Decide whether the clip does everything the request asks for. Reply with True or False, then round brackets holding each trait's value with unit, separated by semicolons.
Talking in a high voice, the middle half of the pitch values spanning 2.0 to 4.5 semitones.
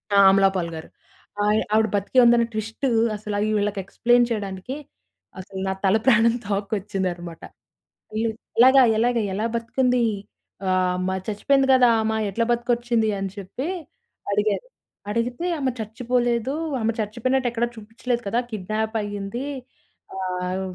True (220 Hz; 3.3 semitones)